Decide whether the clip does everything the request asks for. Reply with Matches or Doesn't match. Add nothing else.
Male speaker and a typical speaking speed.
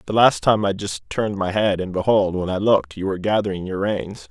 Doesn't match